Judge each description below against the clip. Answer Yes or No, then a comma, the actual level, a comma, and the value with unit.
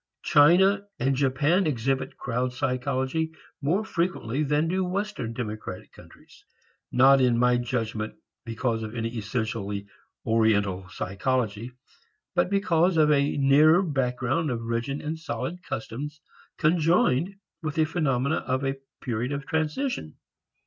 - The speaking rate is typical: No, slow, 125 wpm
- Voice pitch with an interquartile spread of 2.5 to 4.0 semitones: No, average, 5.3 semitones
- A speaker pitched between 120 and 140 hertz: Yes, low, 135 Hz